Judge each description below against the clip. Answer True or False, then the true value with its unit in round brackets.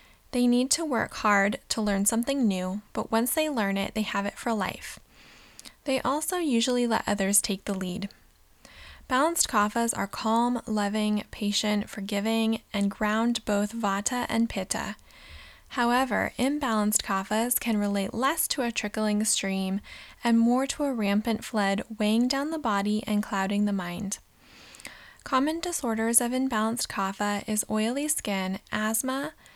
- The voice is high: True (220 Hz)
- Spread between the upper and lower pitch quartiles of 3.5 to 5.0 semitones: False (3.1 semitones)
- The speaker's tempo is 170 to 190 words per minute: False (150 wpm)